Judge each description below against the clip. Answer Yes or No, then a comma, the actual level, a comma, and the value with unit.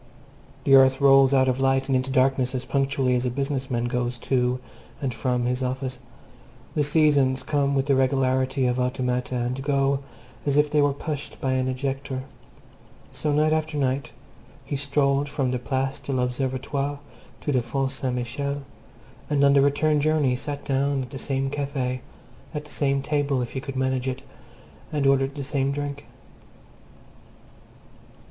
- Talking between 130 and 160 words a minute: No, average, 170 wpm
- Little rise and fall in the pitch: Yes, narrow, 1.6 semitones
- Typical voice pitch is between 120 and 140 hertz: Yes, low, 135 Hz